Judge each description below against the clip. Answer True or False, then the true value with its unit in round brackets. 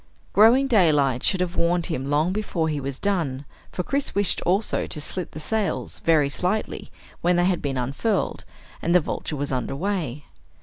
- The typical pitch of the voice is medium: True (170 Hz)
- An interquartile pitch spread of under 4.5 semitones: False (5.3 semitones)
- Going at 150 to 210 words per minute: True (180 wpm)